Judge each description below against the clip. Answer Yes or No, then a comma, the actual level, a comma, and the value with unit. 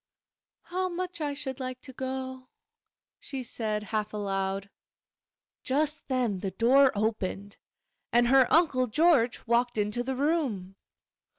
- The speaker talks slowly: Yes, slow, 125 wpm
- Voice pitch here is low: No, very high, 255 Hz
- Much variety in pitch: No, average, 4.7 semitones